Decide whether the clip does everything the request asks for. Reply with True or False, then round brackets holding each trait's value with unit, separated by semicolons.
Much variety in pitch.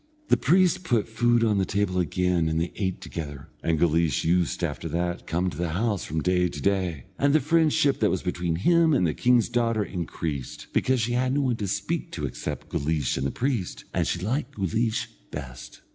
True (6.3 semitones)